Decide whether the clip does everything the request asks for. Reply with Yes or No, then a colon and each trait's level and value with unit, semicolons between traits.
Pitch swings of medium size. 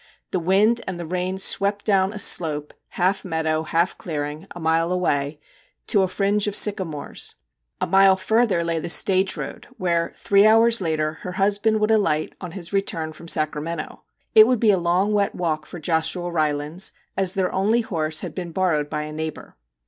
Yes: average, 3.8 semitones